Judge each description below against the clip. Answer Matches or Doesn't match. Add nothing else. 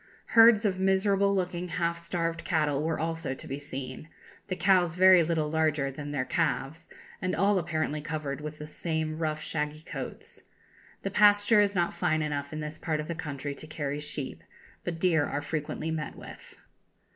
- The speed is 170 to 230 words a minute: Matches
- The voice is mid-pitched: Matches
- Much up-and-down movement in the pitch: Doesn't match